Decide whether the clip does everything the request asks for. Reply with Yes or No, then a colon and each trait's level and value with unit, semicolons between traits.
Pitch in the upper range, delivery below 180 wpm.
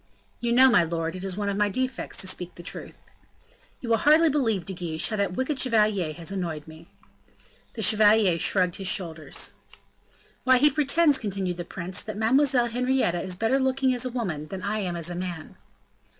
No: high, 200 Hz; average, 195 wpm